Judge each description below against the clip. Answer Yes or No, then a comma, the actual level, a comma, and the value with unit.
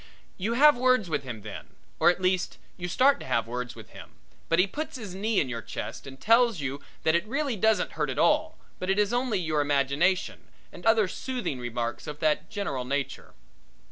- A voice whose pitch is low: No, medium, 180 Hz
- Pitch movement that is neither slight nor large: No, wide, 8.3 semitones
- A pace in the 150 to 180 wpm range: No, fast, 205 wpm